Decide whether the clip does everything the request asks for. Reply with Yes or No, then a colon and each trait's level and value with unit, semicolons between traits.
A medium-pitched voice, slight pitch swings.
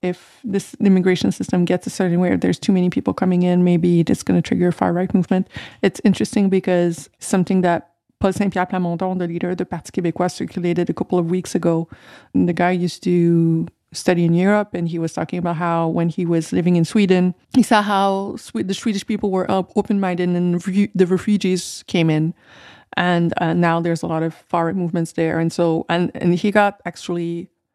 Yes: medium, 180 Hz; narrow, 1.9 semitones